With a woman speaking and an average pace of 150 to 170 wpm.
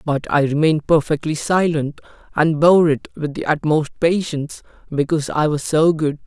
No: male; average, 165 wpm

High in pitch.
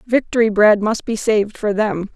Yes: high, 210 Hz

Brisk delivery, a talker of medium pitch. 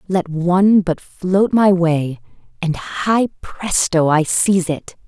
No: average, 140 wpm; medium, 180 Hz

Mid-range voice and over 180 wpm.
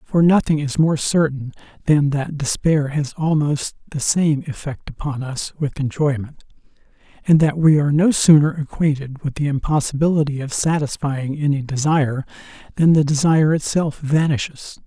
No: medium, 150 Hz; average, 145 wpm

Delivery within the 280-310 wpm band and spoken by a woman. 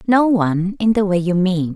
No: fast, 205 wpm; female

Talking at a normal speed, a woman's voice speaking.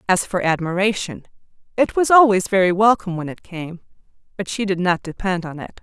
Yes: average, 185 wpm; female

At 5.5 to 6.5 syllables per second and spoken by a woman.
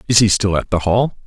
No: 5.9 syllables/s; male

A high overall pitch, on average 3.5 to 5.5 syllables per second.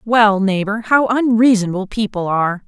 Yes: high, 210 Hz; 5.1 syllables/s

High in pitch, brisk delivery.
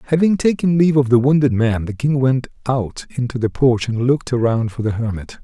No: low, 130 Hz; fast, 220 wpm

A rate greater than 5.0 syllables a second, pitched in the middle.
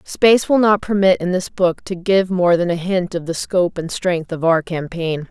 No: 4.8 syllables/s; medium, 180 Hz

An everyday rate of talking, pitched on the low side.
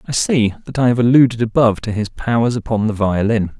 No: fast, 215 wpm; low, 115 Hz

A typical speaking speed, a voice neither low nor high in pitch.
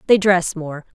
Yes: average, 185 wpm; medium, 175 Hz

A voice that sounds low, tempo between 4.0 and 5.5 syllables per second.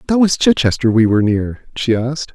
No: low, 130 Hz; 5.7 syllables/s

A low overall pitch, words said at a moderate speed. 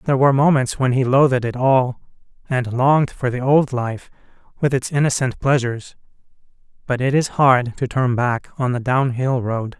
Yes: low, 130 Hz; average, 180 wpm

